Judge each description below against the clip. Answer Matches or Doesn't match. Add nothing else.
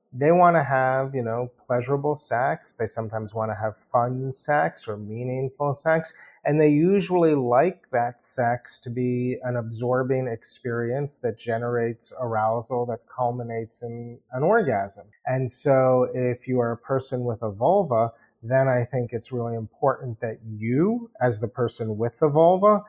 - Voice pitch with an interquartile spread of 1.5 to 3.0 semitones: Matches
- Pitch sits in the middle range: Doesn't match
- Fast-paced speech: Doesn't match